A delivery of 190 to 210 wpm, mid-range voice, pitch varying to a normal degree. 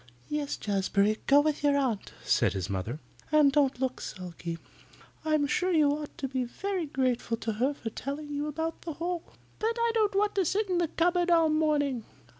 No: average, 195 wpm; very high, 290 Hz; average, 5.0 semitones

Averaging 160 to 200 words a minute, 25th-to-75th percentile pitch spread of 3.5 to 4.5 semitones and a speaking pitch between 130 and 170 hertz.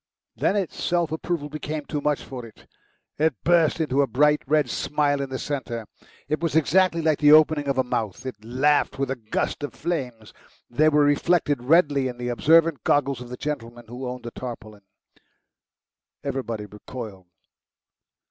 Yes: average, 170 wpm; average, 3.8 semitones; medium, 140 Hz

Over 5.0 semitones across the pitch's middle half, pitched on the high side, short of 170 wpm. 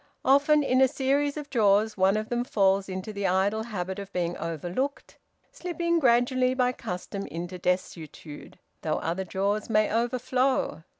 Yes: wide, 5.4 semitones; high, 215 Hz; average, 155 wpm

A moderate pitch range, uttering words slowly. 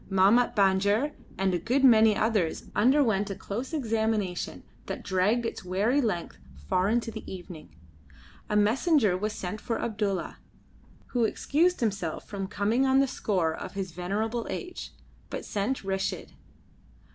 No: average, 3.8 semitones; average, 145 wpm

